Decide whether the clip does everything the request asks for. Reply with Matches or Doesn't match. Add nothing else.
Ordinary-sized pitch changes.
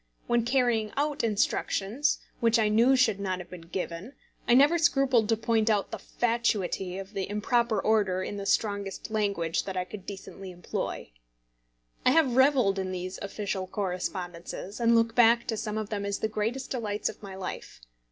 Matches